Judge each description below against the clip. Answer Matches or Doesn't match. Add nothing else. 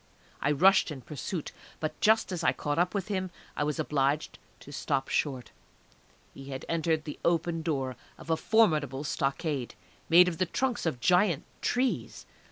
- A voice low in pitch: Doesn't match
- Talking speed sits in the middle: Matches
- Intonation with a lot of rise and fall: Doesn't match